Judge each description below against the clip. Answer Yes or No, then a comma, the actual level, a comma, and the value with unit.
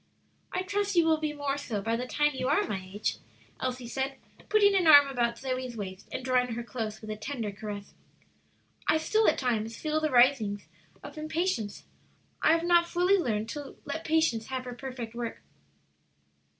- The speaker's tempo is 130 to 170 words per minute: No, average, 185 wpm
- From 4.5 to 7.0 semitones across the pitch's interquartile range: Yes, wide, 5.4 semitones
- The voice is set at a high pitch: Yes, very high, 260 Hz